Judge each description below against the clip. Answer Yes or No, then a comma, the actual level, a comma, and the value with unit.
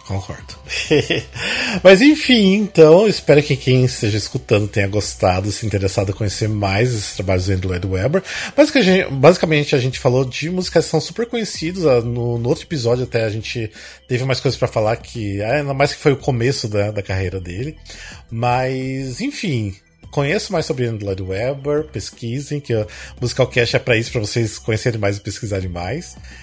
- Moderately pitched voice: No, low, 120 Hz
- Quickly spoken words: No, average, 175 wpm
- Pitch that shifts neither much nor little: No, wide, 6.1 semitones